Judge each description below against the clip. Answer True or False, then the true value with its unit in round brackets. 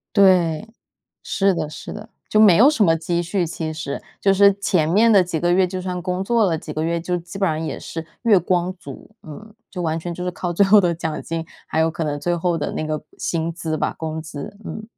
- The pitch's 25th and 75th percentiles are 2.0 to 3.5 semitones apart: True (3.2 semitones)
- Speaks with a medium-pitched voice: True (175 Hz)